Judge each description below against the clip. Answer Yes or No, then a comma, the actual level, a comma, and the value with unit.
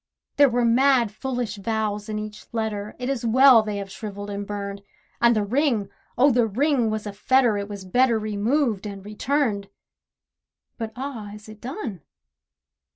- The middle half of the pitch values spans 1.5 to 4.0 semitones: Yes, average, 3.4 semitones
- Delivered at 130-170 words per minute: Yes, average, 165 wpm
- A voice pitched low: No, high, 220 Hz